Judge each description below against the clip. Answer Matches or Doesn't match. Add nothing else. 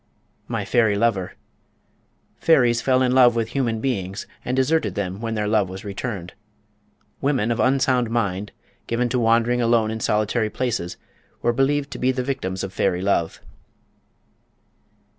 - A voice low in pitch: Matches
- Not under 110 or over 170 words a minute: Matches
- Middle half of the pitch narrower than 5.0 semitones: Matches